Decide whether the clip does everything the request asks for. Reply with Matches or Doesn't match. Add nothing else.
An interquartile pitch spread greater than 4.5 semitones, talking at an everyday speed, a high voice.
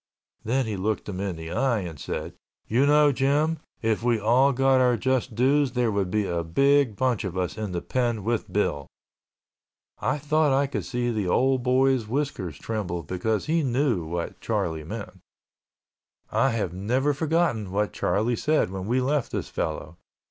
Doesn't match